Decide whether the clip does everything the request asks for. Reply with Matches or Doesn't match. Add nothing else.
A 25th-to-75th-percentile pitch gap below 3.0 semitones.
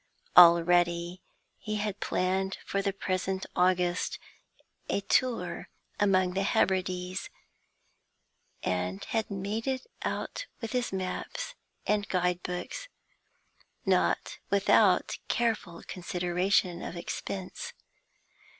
Matches